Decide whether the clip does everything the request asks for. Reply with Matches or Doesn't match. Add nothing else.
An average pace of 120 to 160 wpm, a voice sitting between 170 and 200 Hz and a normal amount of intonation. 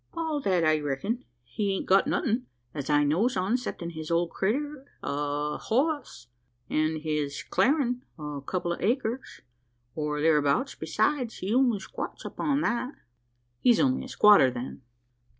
Doesn't match